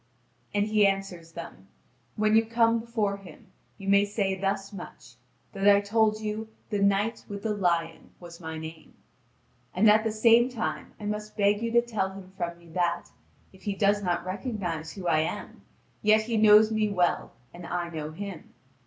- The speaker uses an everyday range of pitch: Yes, average, 3.5 semitones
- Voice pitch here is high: Yes, high, 200 Hz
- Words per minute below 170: No, average, 185 wpm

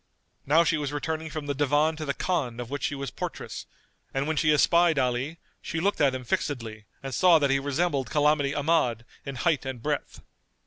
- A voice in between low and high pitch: Yes, medium, 145 Hz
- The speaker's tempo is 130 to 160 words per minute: No, fast, 205 wpm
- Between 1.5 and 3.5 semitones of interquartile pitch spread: Yes, average, 2.9 semitones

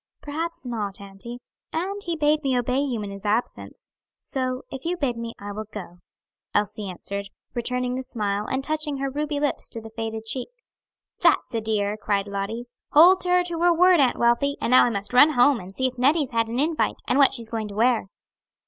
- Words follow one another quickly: Yes, fast, 210 wpm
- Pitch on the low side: No, high, 245 Hz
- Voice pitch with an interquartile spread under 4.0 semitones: No, average, 5.0 semitones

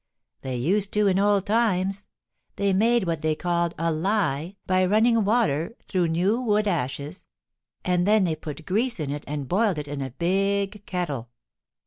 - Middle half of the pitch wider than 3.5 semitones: Yes, average, 4.7 semitones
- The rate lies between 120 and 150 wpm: No, average, 170 wpm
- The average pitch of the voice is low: No, medium, 185 Hz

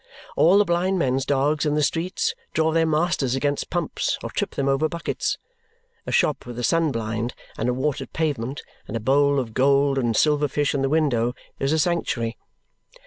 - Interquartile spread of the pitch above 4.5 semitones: No, average, 3.5 semitones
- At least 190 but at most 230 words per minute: Yes, average, 195 wpm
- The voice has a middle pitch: Yes, medium, 145 Hz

